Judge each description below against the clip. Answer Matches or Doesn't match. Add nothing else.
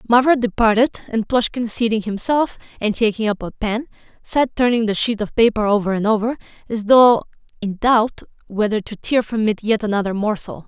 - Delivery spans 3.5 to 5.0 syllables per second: Doesn't match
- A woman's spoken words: Matches